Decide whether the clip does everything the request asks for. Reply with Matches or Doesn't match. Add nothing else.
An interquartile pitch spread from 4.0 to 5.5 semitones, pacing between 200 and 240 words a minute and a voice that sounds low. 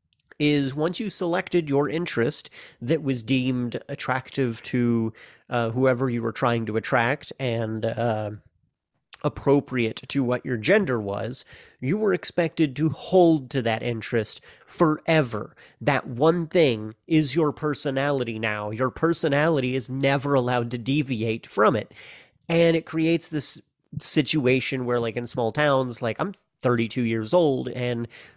Doesn't match